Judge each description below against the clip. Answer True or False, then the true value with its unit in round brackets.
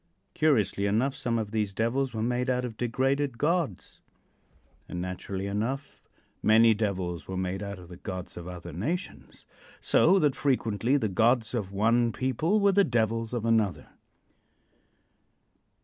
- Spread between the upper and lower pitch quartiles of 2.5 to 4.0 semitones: False (4.8 semitones)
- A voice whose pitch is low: True (115 Hz)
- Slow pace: False (150 wpm)